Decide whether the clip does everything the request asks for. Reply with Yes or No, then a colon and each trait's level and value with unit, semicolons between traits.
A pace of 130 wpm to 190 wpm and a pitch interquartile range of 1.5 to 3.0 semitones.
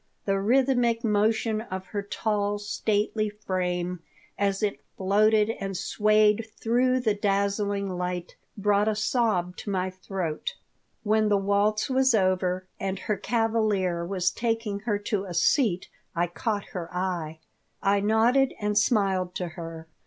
Yes: average, 140 wpm; average, 2.7 semitones